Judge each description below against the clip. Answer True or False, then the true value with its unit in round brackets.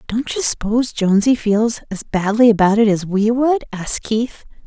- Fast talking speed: False (180 wpm)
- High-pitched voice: True (220 Hz)